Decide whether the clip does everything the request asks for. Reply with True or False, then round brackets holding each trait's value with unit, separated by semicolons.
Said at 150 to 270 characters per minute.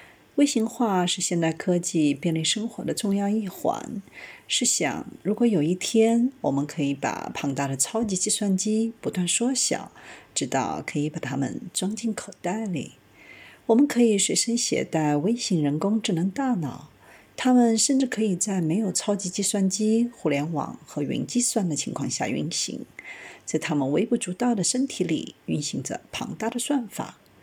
True (250 characters per minute)